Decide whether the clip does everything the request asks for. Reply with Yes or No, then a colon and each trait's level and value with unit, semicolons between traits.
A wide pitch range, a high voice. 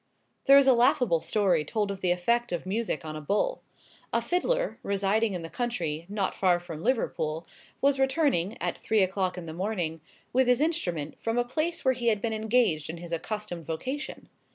Yes: wide, 6.3 semitones; high, 205 Hz